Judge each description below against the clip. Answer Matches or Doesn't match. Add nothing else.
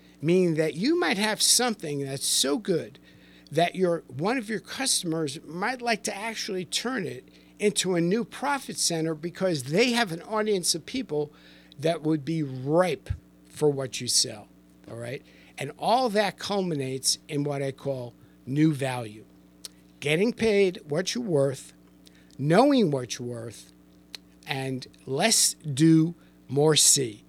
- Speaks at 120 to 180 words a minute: Matches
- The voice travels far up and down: Matches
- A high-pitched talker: Doesn't match